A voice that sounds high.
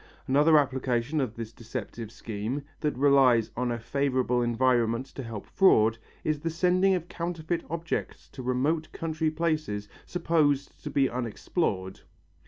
No: low, 135 Hz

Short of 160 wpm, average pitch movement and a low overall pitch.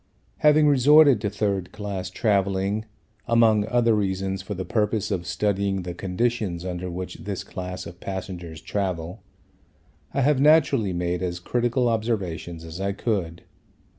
Yes: average, 140 wpm; average, 3.8 semitones; low, 100 Hz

